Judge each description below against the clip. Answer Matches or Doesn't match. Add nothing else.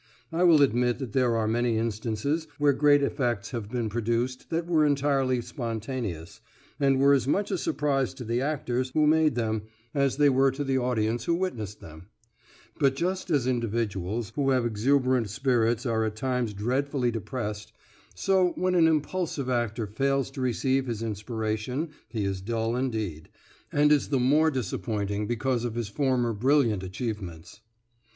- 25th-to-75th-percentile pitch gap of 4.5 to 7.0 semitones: Doesn't match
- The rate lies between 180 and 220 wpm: Doesn't match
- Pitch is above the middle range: Doesn't match